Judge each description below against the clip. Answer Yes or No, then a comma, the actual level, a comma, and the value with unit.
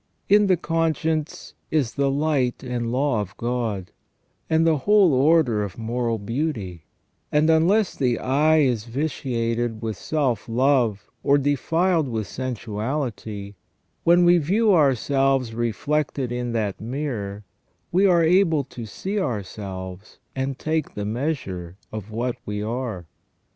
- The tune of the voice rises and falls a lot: Yes, wide, 5.8 semitones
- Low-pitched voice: Yes, low, 130 Hz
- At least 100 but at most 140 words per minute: Yes, slow, 135 wpm